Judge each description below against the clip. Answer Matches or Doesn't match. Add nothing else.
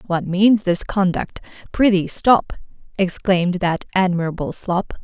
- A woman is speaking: Matches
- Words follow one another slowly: Matches